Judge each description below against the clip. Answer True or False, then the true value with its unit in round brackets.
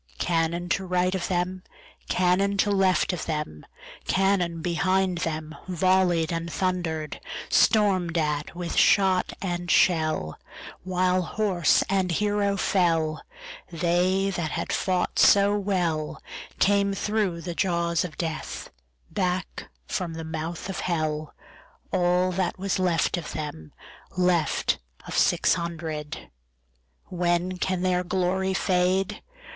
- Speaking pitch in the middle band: True (180 Hz)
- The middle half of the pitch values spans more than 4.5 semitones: False (2.4 semitones)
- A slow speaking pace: True (100 wpm)